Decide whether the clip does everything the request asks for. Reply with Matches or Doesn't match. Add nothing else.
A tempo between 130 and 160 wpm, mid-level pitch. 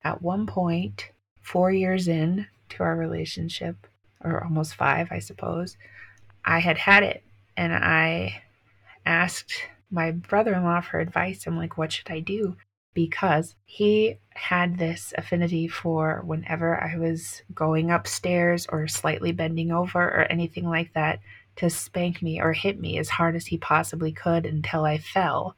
Matches